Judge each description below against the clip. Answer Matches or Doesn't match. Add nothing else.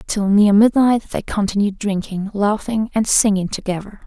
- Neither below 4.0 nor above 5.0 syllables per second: Matches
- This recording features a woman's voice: Matches